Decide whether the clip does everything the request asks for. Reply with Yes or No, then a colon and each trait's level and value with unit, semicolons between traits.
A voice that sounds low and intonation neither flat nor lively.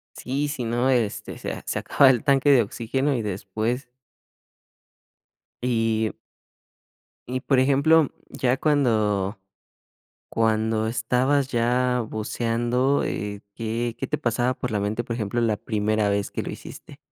Yes: low, 120 Hz; average, 3.0 semitones